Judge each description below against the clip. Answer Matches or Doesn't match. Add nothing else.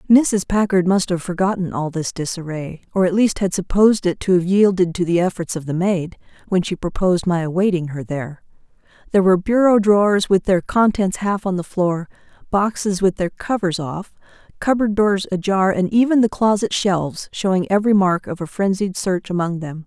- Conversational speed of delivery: Matches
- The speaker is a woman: Matches